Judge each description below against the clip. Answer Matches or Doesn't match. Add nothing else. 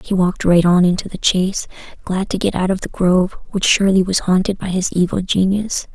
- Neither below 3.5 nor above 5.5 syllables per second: Doesn't match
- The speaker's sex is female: Matches